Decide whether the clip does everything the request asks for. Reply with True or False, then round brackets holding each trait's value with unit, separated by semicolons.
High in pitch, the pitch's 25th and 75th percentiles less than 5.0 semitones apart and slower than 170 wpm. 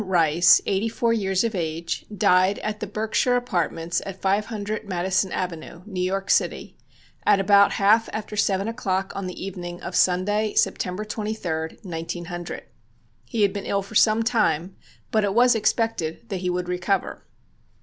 True (195 Hz; 3.1 semitones; 160 wpm)